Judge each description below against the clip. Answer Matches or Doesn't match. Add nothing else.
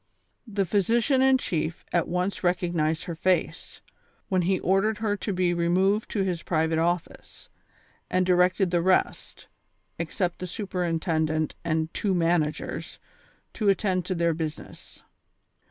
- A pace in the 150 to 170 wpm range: Doesn't match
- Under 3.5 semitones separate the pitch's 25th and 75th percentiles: Matches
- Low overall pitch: Doesn't match